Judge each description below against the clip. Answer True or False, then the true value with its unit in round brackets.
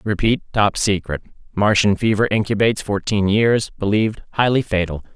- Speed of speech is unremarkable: False (115 wpm)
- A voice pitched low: True (105 Hz)